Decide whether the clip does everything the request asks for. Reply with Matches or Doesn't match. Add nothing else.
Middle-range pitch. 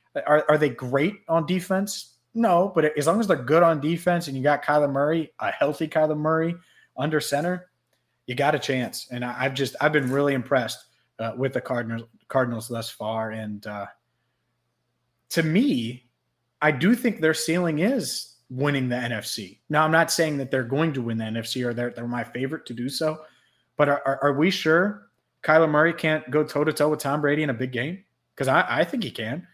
Matches